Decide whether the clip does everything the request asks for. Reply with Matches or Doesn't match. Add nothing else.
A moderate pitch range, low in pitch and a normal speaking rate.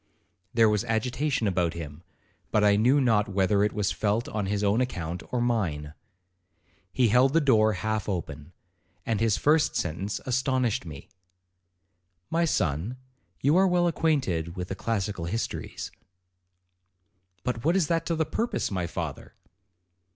Doesn't match